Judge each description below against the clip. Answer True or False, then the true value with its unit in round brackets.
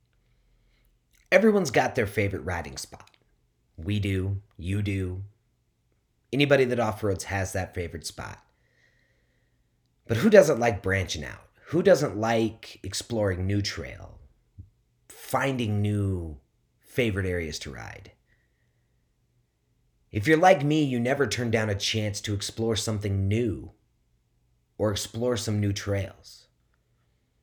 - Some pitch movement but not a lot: True (3.7 semitones)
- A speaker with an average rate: False (120 wpm)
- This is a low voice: True (105 Hz)